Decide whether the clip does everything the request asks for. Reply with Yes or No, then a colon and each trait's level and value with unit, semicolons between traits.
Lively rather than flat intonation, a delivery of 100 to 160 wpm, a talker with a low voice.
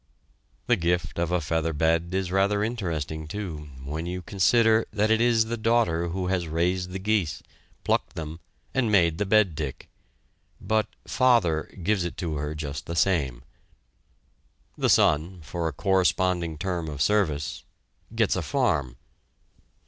No: average, 4.4 semitones; average, 150 wpm; very low, 90 Hz